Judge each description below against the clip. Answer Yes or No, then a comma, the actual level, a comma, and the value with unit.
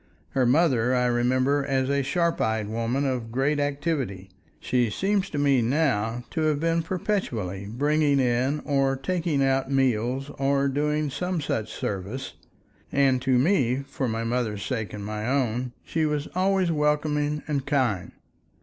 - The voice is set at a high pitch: No, low, 135 Hz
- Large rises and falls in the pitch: No, average, 3.6 semitones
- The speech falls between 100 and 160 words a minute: Yes, average, 150 wpm